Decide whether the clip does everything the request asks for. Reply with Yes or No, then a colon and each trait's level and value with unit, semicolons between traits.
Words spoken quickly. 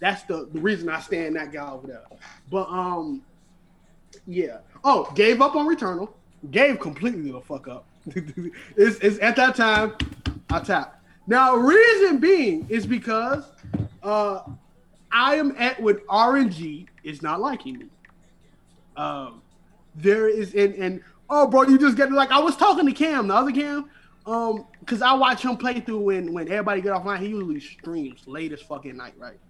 No: average, 170 wpm